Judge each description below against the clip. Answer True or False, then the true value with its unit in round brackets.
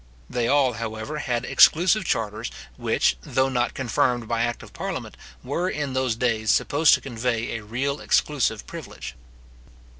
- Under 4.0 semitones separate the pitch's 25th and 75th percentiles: True (3.4 semitones)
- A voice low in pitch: True (125 Hz)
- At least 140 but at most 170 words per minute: True (150 wpm)